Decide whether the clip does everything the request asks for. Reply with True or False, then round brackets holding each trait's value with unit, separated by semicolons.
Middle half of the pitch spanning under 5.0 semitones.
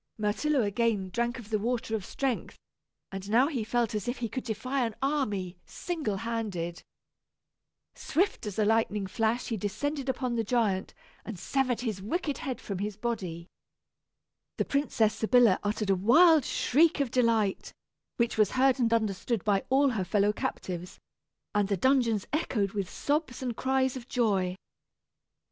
True (4.0 semitones)